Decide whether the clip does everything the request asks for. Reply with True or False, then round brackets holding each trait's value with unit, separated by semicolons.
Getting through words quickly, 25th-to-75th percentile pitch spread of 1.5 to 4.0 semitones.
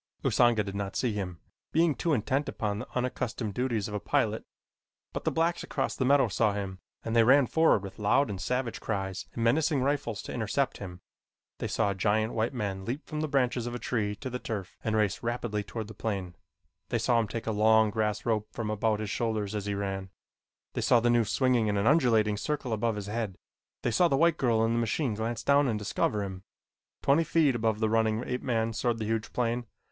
True (225 wpm; 3.2 semitones)